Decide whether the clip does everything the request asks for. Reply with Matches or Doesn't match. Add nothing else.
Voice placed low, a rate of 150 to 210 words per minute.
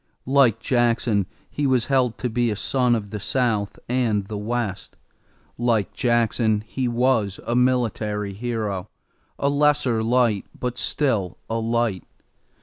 Doesn't match